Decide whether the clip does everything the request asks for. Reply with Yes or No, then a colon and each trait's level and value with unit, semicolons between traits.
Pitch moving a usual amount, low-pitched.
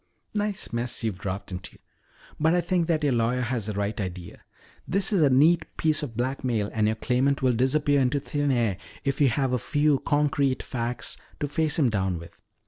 Yes: average, 4.7 semitones; low, 130 Hz